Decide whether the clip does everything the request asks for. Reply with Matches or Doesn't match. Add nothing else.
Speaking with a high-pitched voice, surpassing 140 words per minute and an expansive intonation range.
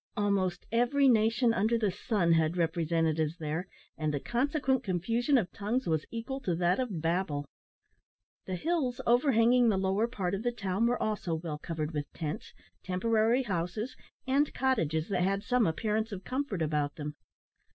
Matches